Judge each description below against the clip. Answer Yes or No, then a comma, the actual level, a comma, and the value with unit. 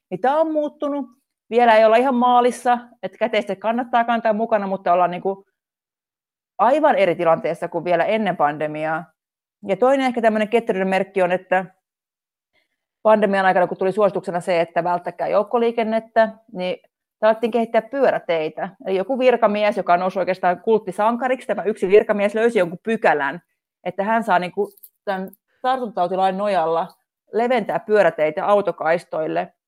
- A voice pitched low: No, high, 205 Hz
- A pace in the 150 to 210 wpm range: No, average, 140 wpm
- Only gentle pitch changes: No, average, 4.2 semitones